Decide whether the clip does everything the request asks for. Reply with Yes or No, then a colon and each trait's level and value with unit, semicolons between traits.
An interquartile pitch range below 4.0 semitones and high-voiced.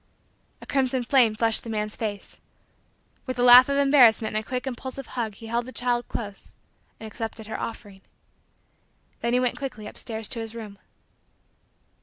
Yes: narrow, 2.5 semitones; high, 235 Hz